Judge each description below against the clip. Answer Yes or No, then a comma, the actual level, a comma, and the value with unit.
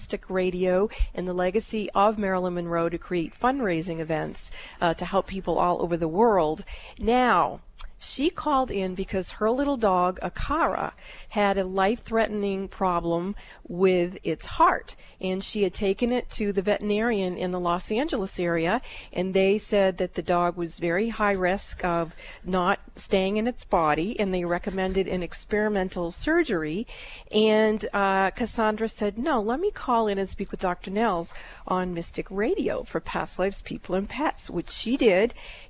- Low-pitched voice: No, high, 195 Hz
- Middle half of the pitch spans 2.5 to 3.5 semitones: Yes, average, 3.1 semitones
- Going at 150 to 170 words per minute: Yes, average, 165 wpm